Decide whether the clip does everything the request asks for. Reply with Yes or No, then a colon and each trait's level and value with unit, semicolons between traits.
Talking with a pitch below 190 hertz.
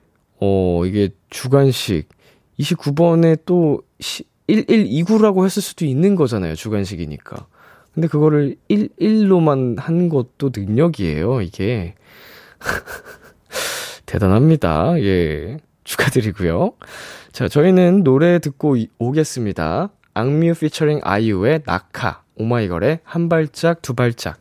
Yes: medium, 140 Hz